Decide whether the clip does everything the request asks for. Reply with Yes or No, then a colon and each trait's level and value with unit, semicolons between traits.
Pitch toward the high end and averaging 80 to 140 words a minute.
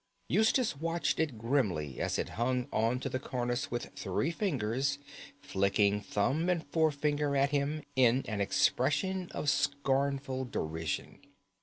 No: low, 135 Hz; slow, 135 wpm